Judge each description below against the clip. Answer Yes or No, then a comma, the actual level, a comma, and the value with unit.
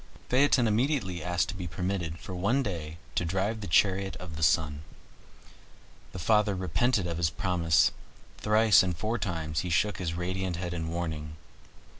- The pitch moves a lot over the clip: No, average, 3.8 semitones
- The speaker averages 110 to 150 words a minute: No, average, 165 wpm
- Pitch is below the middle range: Yes, very low, 90 Hz